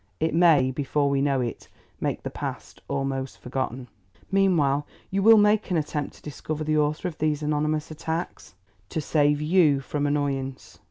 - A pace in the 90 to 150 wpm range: No, average, 165 wpm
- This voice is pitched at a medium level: Yes, medium, 150 Hz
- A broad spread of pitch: No, narrow, 2.6 semitones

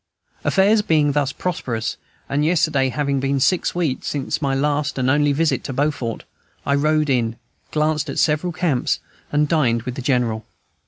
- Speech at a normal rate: Yes, average, 165 wpm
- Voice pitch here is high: No, medium, 145 Hz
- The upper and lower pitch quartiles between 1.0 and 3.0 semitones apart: Yes, average, 2.7 semitones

